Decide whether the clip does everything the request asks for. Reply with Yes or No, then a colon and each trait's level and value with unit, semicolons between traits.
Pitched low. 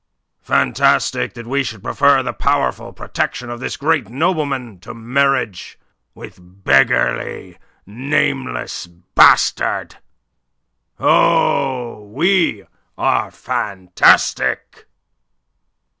Yes: low, 125 Hz